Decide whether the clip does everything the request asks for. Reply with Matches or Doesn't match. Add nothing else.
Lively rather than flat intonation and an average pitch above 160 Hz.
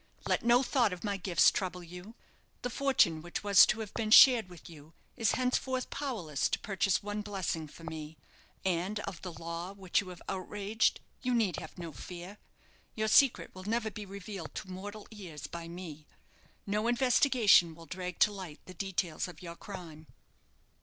Doesn't match